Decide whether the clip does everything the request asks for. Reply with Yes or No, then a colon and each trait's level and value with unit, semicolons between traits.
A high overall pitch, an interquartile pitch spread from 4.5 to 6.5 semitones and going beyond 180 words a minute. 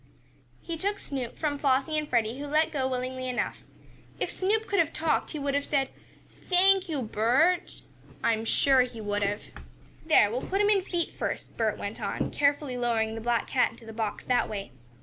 Yes: very high, 270 Hz; average, 5.3 semitones; average, 200 wpm